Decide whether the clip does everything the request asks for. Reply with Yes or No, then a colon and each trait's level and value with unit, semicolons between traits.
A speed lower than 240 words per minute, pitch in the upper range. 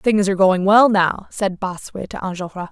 Yes: average, 200 wpm; high, 195 Hz